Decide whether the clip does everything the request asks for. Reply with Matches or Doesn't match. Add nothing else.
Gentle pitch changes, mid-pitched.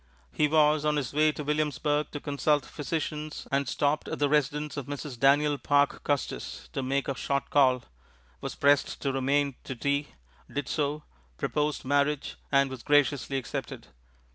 Matches